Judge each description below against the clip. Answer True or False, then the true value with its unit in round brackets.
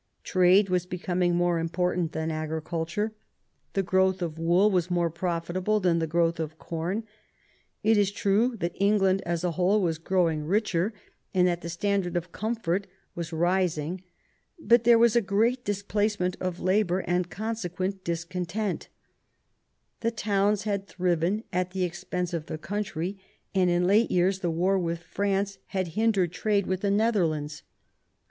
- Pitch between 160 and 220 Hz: True (185 Hz)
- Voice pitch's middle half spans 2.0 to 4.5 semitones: True (2.9 semitones)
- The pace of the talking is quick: False (155 wpm)